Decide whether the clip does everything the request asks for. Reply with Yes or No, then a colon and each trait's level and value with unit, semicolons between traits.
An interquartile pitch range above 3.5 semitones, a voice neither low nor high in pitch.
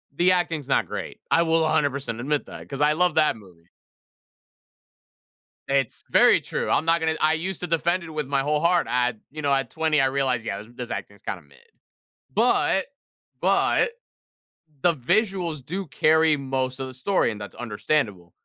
Yes: average, 4.5 semitones; medium, 150 Hz